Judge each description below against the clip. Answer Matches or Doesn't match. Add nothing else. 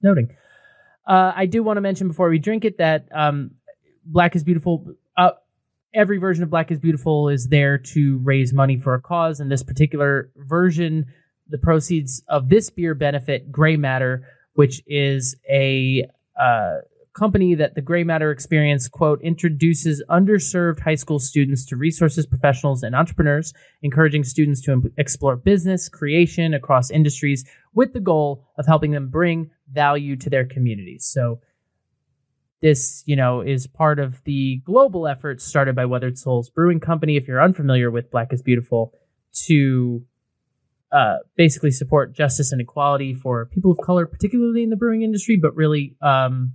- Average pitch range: Matches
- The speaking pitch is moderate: Matches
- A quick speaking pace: Doesn't match